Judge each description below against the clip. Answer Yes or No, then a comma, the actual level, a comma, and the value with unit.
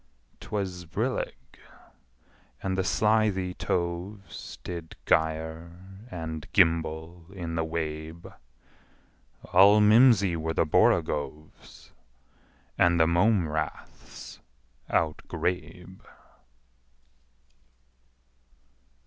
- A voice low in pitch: Yes, very low, 85 Hz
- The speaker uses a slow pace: Yes, slow, 70 wpm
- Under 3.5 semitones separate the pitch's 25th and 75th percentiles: Yes, average, 2.8 semitones